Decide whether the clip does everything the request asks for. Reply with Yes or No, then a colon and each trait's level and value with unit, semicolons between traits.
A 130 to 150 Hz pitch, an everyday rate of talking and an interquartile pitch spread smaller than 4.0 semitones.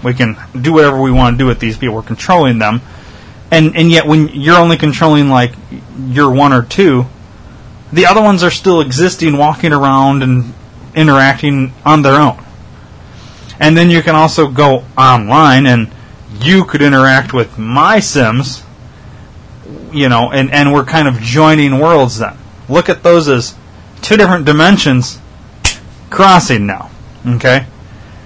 No: low, 135 Hz; average, 155 wpm; average, 4.9 semitones